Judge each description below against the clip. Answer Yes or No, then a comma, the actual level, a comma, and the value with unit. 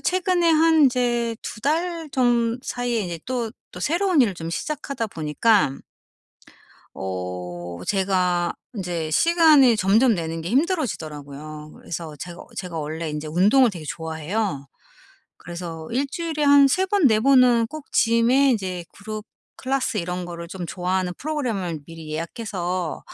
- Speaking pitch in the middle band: No, high, 205 Hz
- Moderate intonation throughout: No, wide, 8.1 semitones